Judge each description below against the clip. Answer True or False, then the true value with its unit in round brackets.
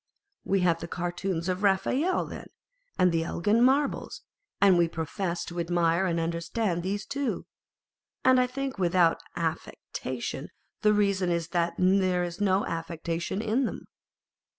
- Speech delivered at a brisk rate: False (150 wpm)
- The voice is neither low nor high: True (180 Hz)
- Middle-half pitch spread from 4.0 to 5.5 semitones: False (3.3 semitones)